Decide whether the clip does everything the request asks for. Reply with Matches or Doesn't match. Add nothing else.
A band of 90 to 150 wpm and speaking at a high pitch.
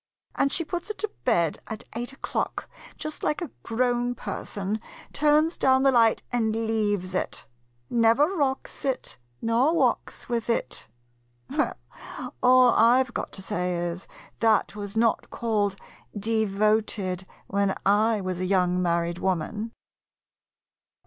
Matches